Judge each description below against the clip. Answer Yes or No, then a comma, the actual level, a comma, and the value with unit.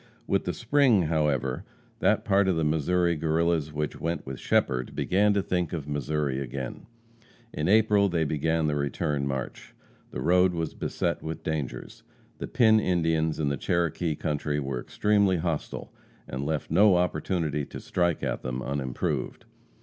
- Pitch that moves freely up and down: No, average, 3.5 semitones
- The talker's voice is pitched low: Yes, very low, 80 Hz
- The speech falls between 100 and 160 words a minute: Yes, average, 155 wpm